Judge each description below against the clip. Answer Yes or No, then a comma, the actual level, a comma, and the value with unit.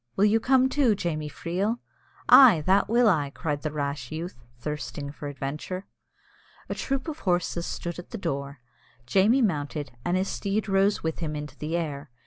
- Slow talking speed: No, average, 175 wpm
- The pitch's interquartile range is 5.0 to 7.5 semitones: Yes, wide, 5.6 semitones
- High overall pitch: No, medium, 170 Hz